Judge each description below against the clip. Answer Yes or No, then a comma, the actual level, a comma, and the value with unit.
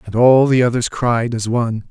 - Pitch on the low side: Yes, low, 120 Hz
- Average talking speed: No, fast, 220 wpm